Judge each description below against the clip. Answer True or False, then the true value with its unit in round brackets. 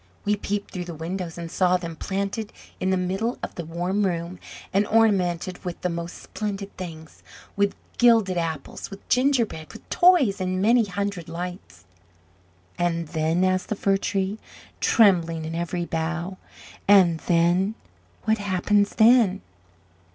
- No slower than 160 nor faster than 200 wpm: False (145 wpm)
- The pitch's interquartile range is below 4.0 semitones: True (3.0 semitones)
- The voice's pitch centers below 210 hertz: True (185 Hz)